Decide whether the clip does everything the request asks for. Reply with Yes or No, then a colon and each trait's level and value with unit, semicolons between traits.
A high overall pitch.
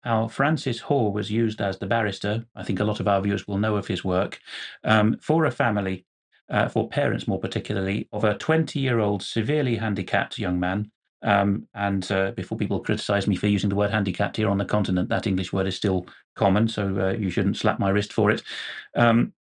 No: low, 105 Hz